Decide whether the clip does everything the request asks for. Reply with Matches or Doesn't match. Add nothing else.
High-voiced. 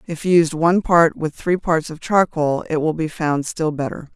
Doesn't match